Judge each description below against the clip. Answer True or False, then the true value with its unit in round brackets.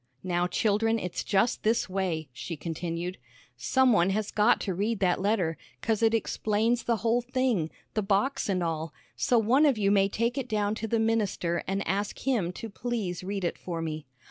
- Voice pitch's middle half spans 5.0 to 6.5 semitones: False (4.2 semitones)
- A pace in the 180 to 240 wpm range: True (195 wpm)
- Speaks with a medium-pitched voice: False (205 Hz)